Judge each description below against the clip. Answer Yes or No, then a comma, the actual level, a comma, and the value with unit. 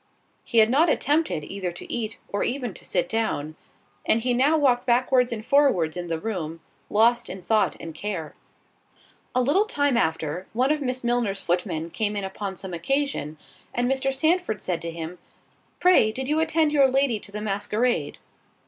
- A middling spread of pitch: No, wide, 6.6 semitones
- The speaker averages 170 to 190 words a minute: Yes, average, 180 wpm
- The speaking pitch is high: Yes, high, 225 Hz